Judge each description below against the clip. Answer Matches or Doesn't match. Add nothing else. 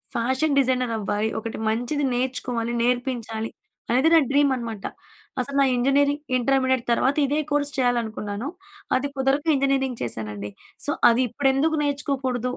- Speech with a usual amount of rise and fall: Matches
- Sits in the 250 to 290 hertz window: Matches